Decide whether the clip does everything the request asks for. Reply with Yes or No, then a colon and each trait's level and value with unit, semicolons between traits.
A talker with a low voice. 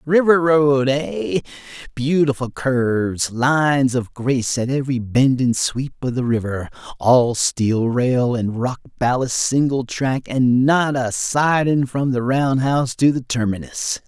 Yes: low, 130 Hz